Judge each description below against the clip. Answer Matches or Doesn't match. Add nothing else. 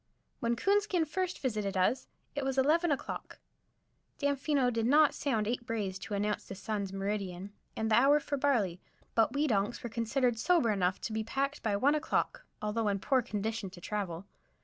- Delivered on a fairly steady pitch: Doesn't match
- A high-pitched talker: Matches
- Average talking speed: Matches